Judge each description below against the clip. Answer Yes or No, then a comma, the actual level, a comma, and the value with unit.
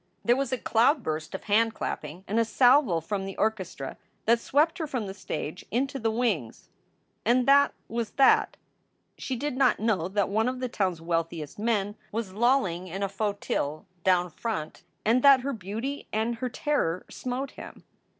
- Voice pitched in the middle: No, high, 220 Hz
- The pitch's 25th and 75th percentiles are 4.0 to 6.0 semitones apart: Yes, average, 5.2 semitones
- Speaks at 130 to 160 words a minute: No, average, 175 wpm